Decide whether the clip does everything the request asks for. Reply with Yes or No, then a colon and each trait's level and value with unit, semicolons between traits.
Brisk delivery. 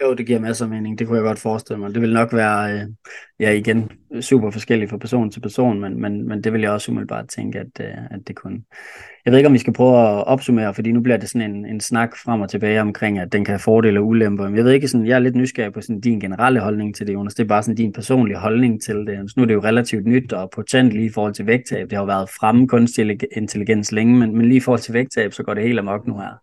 Yes: fast, 280 wpm